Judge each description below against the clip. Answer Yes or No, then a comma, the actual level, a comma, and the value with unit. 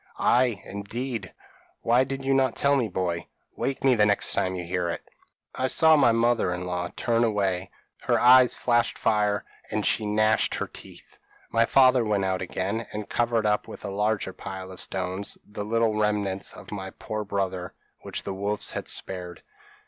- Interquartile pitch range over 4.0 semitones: No, average, 3.7 semitones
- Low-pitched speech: Yes, low, 105 Hz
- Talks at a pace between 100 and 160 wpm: No, average, 185 wpm